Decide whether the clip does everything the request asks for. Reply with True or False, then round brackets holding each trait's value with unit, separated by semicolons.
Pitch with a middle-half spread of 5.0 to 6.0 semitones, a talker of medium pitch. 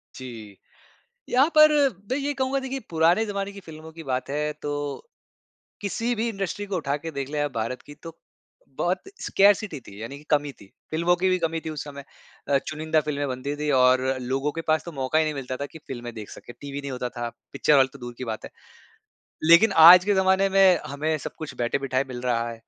True (5.6 semitones; 150 Hz)